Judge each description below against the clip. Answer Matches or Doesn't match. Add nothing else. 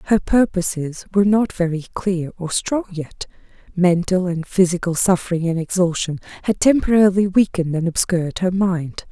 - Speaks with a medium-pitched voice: Matches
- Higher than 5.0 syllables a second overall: Matches